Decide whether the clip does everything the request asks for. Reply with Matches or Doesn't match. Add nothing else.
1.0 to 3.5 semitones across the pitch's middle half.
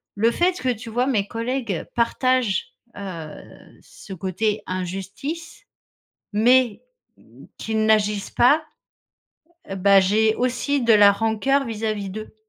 Doesn't match